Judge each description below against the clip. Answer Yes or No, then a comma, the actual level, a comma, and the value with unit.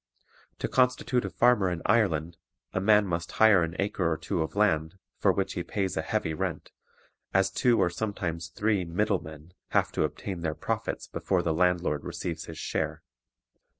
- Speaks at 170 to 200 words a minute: Yes, average, 180 wpm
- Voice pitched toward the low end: Yes, very low, 90 Hz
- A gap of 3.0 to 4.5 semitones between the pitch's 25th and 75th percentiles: Yes, average, 4.0 semitones